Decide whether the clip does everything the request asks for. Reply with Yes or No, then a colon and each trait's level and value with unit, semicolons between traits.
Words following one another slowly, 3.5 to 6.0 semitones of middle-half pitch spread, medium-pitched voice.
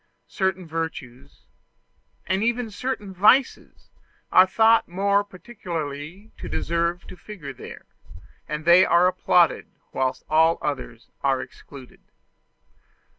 Yes: slow, 110 wpm; average, 5.0 semitones; medium, 175 Hz